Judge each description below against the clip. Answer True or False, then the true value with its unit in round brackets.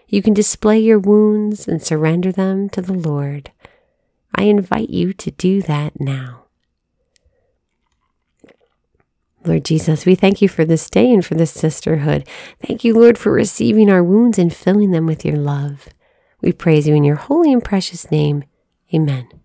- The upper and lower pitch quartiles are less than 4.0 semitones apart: False (5.4 semitones)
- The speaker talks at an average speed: True (165 wpm)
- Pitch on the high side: False (180 Hz)